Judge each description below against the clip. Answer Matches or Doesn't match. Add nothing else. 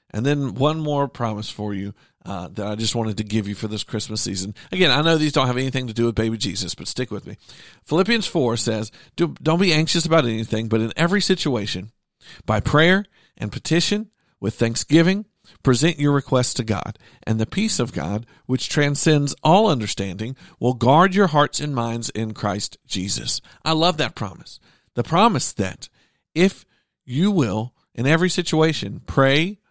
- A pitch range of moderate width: Doesn't match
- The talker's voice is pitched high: Doesn't match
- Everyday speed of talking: Matches